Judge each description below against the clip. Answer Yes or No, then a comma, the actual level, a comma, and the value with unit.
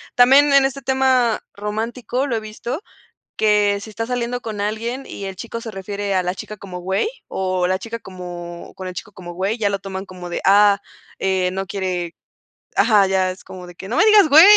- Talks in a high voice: Yes, high, 205 Hz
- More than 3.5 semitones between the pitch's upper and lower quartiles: Yes, average, 4.0 semitones